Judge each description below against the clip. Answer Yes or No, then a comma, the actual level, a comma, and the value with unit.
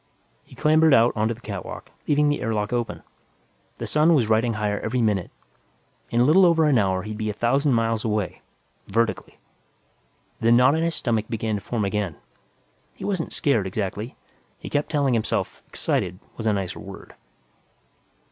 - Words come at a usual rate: Yes, average, 175 wpm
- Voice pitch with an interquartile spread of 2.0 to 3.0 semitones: No, average, 5.0 semitones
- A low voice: Yes, low, 115 Hz